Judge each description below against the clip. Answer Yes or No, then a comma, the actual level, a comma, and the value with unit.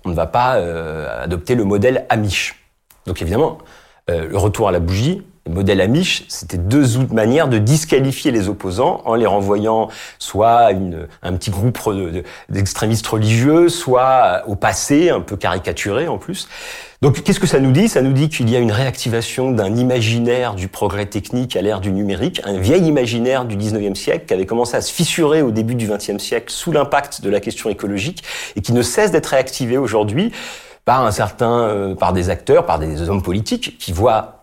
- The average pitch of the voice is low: Yes, low, 110 Hz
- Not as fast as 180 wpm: No, average, 200 wpm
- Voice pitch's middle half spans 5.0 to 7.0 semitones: No, average, 4.6 semitones